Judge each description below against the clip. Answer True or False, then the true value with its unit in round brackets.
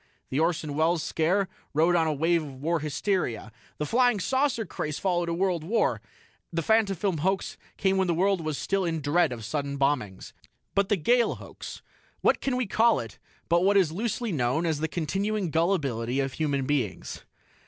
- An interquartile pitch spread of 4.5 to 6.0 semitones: True (4.9 semitones)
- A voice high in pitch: False (170 Hz)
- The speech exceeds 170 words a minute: True (180 wpm)